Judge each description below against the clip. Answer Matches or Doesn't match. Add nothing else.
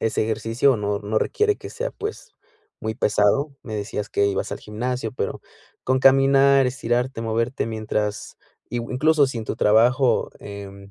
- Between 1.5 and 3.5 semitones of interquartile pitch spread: Doesn't match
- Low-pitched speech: Matches